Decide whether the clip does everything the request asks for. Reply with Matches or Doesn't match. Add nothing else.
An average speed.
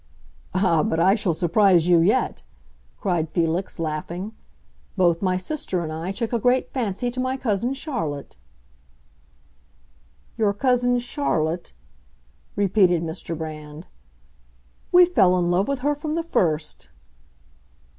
Doesn't match